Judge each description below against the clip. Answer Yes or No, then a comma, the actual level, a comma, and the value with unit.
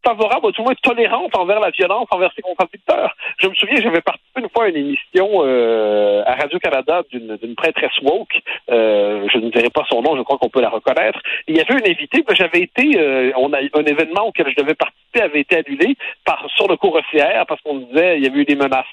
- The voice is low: No, medium, 160 Hz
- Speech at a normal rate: No, fast, 245 wpm